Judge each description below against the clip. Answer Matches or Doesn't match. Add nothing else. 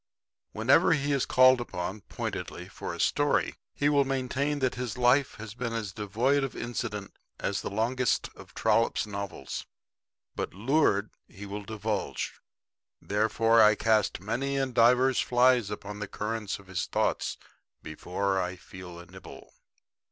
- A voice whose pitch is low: Matches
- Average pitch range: Matches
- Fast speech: Doesn't match